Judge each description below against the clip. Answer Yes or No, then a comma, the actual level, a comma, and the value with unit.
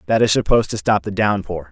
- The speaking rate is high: Yes, fast, 245 wpm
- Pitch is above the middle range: No, low, 100 Hz